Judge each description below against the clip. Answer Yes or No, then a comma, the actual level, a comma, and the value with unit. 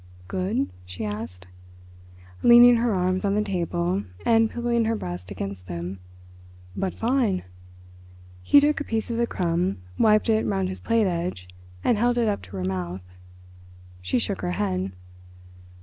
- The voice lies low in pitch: No, medium, 185 Hz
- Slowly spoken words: No, average, 155 wpm